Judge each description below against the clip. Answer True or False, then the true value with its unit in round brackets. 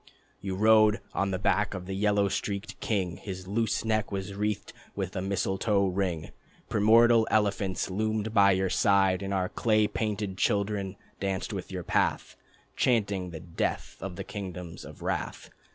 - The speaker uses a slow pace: False (160 wpm)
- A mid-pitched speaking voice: False (100 Hz)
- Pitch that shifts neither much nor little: False (2.1 semitones)